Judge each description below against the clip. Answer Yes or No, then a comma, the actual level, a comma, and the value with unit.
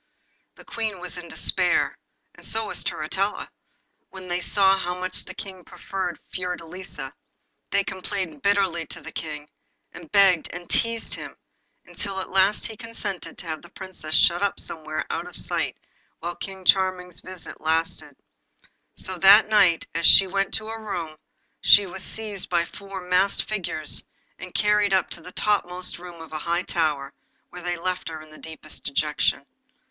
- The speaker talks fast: No, average, 170 wpm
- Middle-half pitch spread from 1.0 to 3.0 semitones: Yes, narrow, 2.6 semitones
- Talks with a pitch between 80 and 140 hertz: No, medium, 185 Hz